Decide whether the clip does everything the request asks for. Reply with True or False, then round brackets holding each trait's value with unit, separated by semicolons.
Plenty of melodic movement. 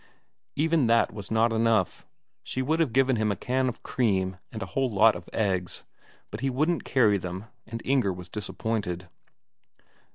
False (4.8 semitones)